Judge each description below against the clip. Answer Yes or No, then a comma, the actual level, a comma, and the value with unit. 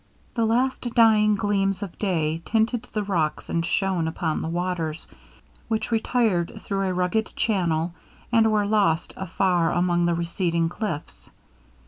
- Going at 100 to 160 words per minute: Yes, average, 140 wpm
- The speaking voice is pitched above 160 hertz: Yes, medium, 185 Hz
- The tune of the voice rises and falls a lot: No, average, 4.2 semitones